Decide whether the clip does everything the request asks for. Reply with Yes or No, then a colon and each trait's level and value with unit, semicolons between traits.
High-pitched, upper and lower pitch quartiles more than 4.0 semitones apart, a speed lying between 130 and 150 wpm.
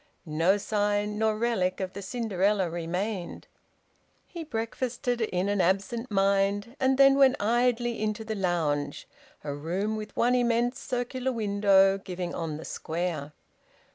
Yes: high, 205 Hz; average, 4.4 semitones; average, 140 wpm